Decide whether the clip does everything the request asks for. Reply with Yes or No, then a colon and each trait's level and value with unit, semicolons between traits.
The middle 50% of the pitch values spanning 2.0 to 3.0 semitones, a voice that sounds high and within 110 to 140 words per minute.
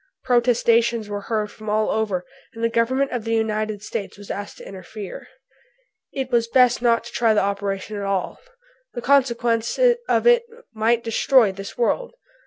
No: narrow, 2.5 semitones; high, 225 Hz; average, 170 wpm